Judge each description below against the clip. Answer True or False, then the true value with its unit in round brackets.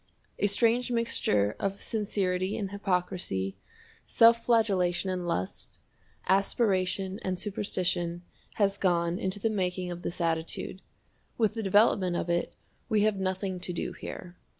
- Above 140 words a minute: False (135 wpm)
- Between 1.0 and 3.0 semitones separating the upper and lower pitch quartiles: True (2.7 semitones)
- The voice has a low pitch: False (190 Hz)